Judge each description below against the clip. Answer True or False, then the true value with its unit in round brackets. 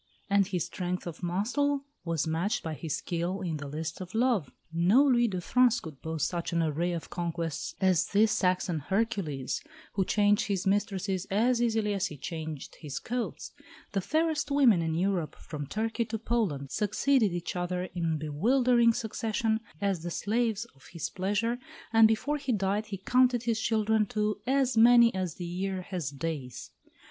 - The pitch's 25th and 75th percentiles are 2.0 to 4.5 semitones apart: False (5.1 semitones)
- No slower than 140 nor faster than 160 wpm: False (175 wpm)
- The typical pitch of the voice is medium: False (195 Hz)